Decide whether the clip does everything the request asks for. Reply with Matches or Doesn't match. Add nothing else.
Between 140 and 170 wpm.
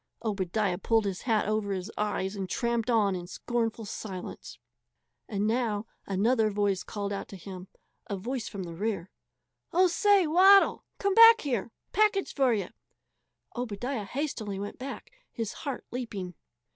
Matches